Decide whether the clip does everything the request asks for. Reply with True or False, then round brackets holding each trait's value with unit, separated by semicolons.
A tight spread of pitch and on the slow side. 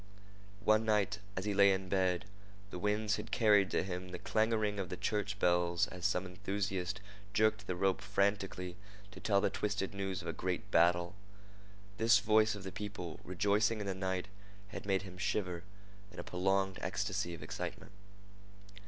False (2.3 semitones; 170 wpm)